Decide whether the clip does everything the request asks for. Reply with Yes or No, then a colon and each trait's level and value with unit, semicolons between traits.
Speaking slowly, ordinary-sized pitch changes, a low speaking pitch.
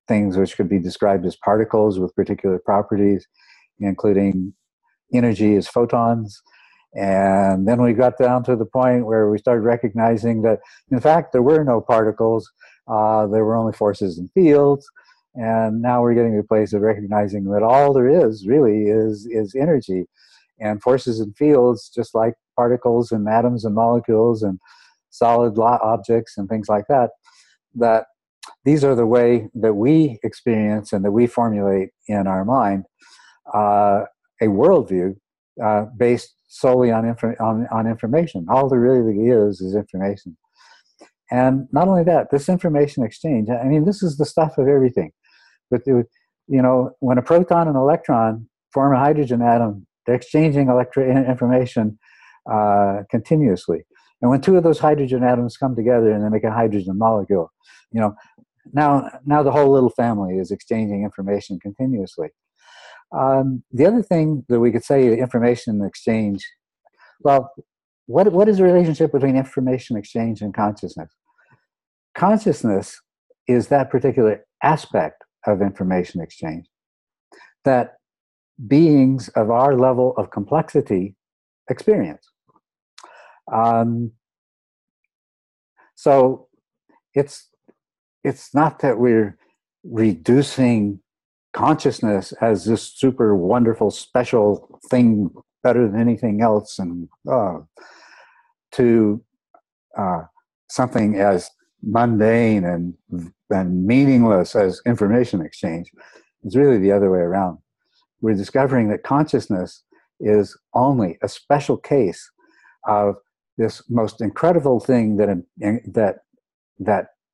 Yes: slow, 130 wpm; average, 3.9 semitones; low, 115 Hz